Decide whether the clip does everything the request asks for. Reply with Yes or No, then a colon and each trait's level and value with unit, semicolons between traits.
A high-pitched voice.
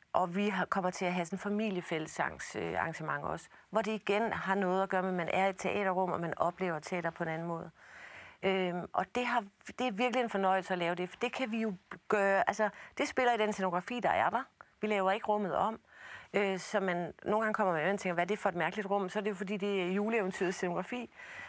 Yes: high, 195 Hz